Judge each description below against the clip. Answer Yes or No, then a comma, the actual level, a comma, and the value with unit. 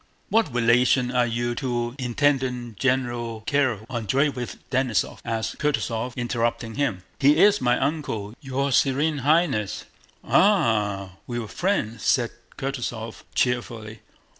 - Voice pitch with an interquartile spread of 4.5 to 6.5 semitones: No, average, 3.1 semitones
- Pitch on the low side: Yes, low, 125 Hz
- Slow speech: Yes, slow, 115 wpm